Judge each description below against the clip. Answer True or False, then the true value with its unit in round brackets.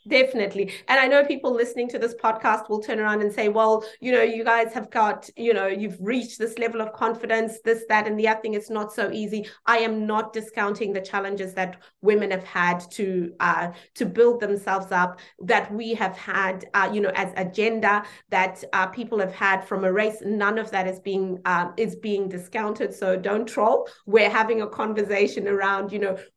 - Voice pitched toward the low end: False (210 Hz)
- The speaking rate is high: True (210 wpm)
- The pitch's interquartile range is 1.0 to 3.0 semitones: True (2.5 semitones)